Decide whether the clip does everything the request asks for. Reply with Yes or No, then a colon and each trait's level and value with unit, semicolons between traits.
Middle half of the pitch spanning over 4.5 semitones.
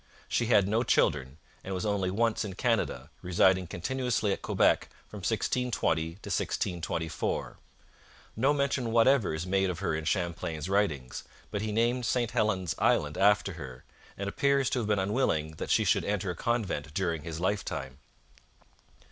Yes: wide, 5.6 semitones